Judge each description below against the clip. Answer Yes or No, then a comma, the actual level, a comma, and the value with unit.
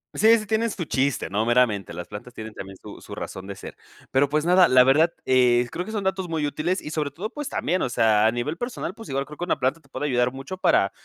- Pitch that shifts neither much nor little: No, wide, 6.8 semitones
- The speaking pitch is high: No, medium, 140 Hz